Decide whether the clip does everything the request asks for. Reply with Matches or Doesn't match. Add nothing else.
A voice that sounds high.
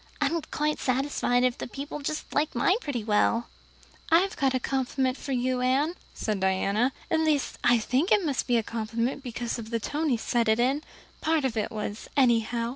Matches